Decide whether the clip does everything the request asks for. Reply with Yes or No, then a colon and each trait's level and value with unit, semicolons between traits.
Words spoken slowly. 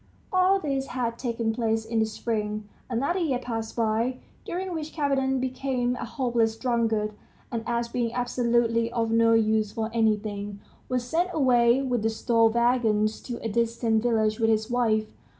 No: average, 165 wpm